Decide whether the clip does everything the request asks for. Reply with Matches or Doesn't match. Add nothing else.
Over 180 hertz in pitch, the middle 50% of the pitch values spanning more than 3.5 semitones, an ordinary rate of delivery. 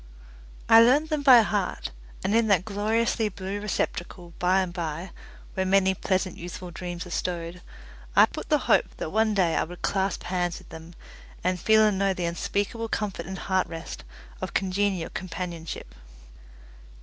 Doesn't match